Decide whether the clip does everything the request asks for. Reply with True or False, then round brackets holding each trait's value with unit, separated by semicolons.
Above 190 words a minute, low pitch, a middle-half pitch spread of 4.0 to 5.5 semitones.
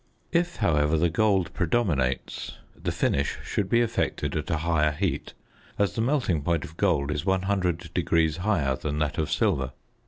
False (160 wpm; 85 Hz; 4.7 semitones)